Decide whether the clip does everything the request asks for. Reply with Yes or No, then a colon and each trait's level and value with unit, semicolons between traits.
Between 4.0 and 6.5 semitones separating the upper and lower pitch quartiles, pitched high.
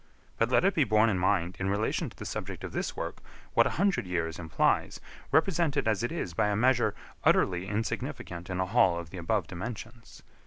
No: average, 4.9 semitones; low, 105 Hz